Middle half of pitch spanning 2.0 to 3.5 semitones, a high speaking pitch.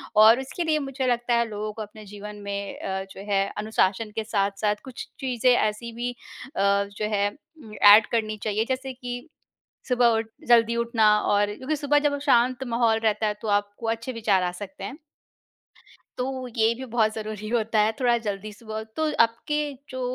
Yes: average, 2.9 semitones; high, 225 Hz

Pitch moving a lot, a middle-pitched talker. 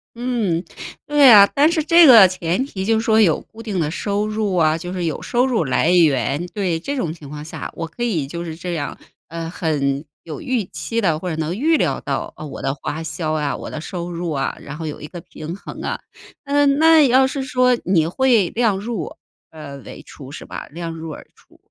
Yes: wide, 6.8 semitones; medium, 175 Hz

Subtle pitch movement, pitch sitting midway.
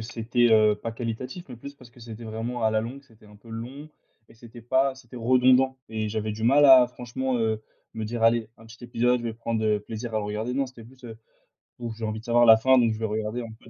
No: narrow, 2.0 semitones; low, 115 Hz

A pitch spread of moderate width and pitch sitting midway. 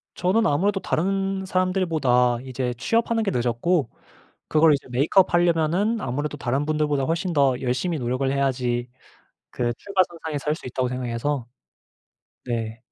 No: wide, 6.4 semitones; medium, 145 Hz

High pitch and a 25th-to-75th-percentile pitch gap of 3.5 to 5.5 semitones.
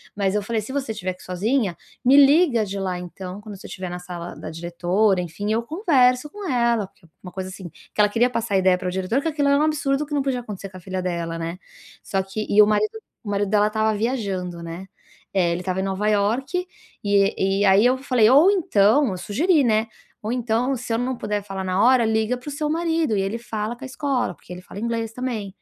Yes: high, 215 Hz; average, 5.0 semitones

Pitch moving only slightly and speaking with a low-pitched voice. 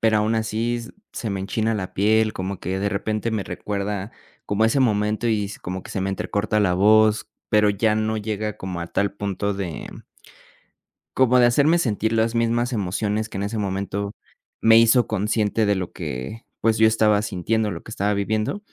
Yes: narrow, 1.9 semitones; low, 105 Hz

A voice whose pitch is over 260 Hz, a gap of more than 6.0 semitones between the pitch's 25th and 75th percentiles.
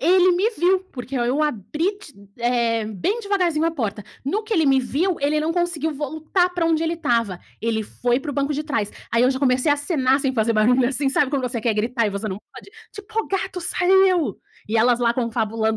Yes: very high, 275 Hz; wide, 6.5 semitones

